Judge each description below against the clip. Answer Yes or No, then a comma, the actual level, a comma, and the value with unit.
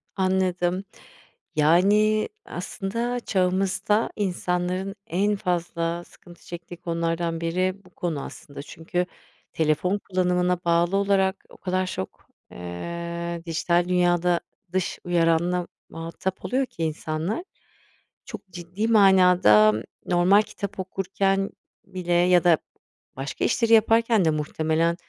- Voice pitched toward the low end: No, medium, 180 Hz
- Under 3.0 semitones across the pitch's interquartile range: Yes, narrow, 2.4 semitones